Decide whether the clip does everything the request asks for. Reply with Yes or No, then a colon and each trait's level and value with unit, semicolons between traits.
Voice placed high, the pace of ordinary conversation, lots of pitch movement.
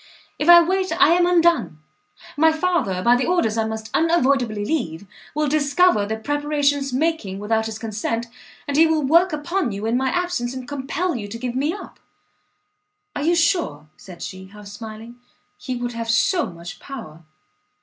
Yes: very high, 260 Hz; average, 175 wpm; wide, 6.6 semitones